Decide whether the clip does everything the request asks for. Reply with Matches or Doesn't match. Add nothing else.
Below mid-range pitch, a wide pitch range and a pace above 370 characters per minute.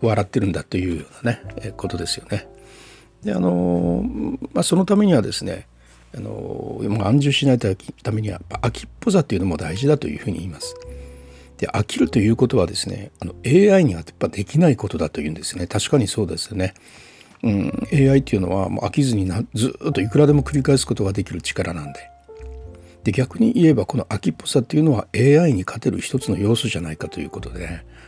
Matches